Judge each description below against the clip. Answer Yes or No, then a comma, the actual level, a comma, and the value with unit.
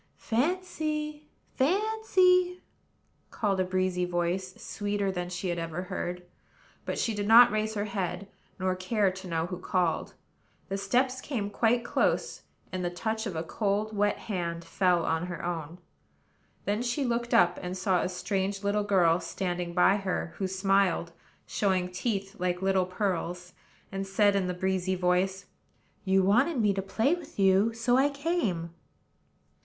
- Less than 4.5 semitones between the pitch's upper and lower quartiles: Yes, average, 3.6 semitones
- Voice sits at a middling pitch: No, high, 195 Hz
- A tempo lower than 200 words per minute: Yes, average, 160 wpm